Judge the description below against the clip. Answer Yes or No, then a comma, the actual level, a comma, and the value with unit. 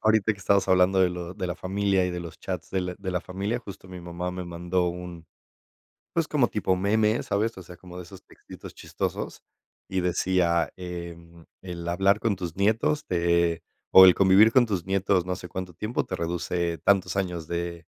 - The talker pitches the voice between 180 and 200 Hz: No, very low, 90 Hz